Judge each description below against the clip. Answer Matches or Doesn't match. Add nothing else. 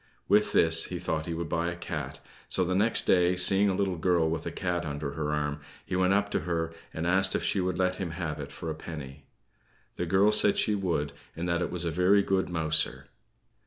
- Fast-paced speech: Matches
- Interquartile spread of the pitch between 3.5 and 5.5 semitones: Doesn't match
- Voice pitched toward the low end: Matches